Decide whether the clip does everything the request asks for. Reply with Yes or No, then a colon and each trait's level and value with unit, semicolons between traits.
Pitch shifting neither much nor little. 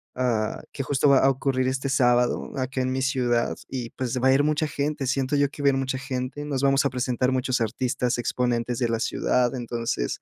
No: narrow, 1.8 semitones